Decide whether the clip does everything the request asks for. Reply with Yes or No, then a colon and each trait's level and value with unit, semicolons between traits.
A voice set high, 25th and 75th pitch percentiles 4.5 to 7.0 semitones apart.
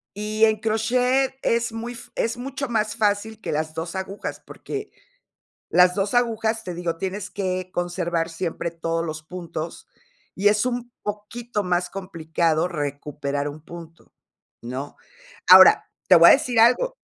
Yes: high, 195 Hz; average, 5.3 semitones